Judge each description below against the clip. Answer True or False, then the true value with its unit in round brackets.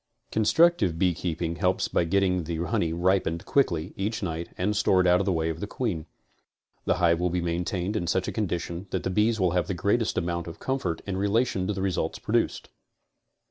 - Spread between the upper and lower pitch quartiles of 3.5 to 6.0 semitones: False (3.0 semitones)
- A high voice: False (90 Hz)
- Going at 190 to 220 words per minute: True (200 wpm)